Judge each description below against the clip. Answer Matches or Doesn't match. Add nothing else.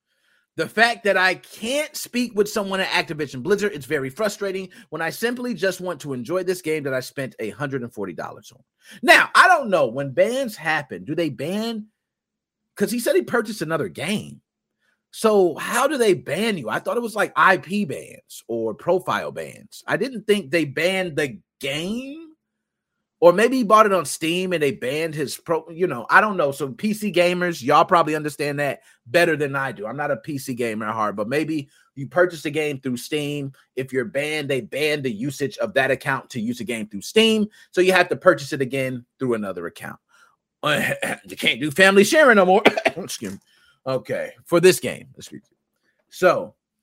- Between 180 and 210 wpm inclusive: Matches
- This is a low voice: Doesn't match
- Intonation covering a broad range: Matches